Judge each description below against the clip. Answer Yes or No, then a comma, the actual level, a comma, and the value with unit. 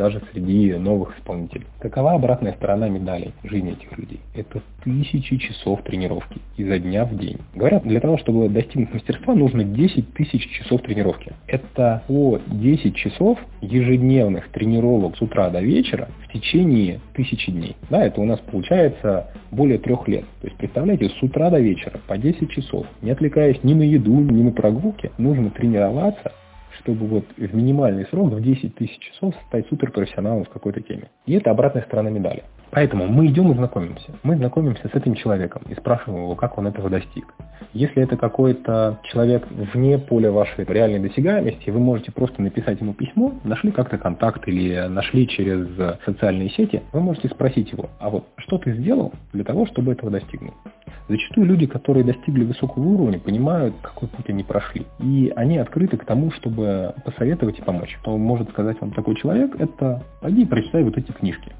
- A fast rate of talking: Yes, fast, 170 wpm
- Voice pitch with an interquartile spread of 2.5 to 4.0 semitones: No, average, 4.9 semitones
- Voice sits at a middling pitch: No, low, 115 Hz